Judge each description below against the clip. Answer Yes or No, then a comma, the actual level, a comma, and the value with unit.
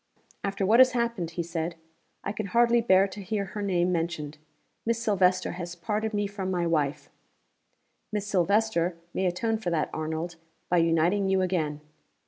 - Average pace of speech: Yes, average, 165 wpm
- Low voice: No, medium, 185 Hz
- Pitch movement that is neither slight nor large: Yes, average, 3.5 semitones